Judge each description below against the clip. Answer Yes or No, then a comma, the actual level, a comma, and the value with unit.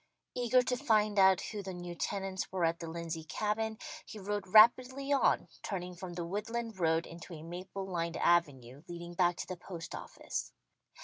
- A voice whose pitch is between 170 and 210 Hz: Yes, medium, 185 Hz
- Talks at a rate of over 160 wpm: Yes, average, 180 wpm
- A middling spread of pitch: Yes, average, 3.8 semitones